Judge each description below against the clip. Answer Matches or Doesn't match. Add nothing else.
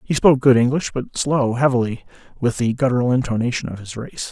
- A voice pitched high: Doesn't match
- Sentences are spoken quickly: Doesn't match